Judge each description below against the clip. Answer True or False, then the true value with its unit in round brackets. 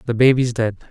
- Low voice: True (120 Hz)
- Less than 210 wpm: True (200 wpm)